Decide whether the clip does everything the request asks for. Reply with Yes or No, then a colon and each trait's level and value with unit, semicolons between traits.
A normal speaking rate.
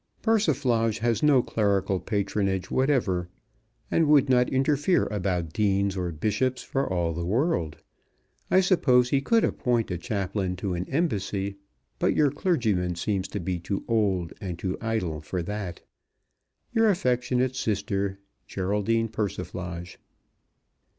No: slow, 130 wpm